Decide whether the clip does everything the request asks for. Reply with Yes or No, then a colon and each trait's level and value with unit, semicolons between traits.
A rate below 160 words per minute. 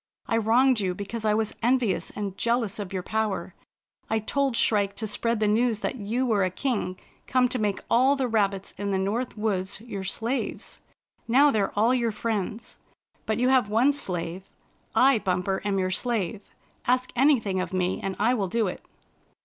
No: average, 185 wpm